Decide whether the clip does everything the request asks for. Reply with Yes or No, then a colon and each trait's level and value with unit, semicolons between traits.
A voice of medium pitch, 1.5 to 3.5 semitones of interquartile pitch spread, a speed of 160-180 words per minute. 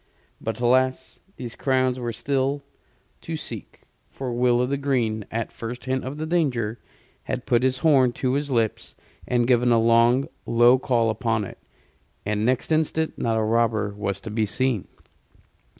No: low, 120 Hz; narrow, 2.4 semitones; average, 165 wpm